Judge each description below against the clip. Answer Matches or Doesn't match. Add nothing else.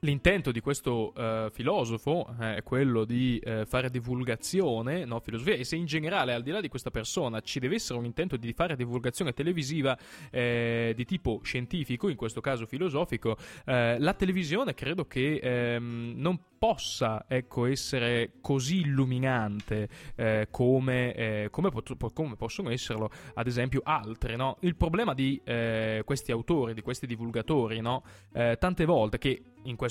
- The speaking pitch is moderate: Doesn't match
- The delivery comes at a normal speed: Matches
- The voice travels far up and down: Doesn't match